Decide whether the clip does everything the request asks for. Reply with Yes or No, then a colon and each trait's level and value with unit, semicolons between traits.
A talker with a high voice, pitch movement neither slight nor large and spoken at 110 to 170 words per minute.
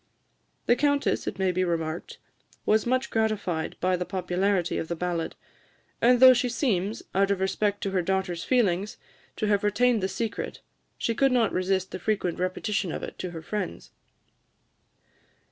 Yes: high, 195 Hz; average, 3.7 semitones; average, 165 wpm